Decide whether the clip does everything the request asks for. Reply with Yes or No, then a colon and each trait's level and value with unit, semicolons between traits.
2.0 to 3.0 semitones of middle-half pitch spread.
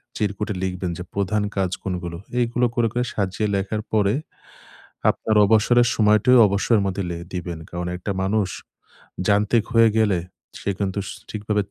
Yes: narrow, 2.5 semitones